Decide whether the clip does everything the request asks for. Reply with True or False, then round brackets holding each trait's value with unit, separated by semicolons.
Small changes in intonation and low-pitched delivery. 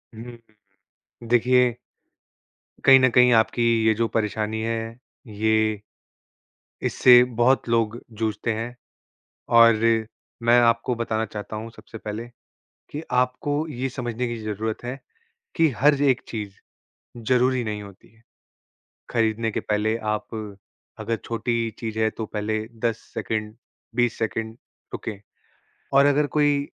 True (2.1 semitones; 115 Hz)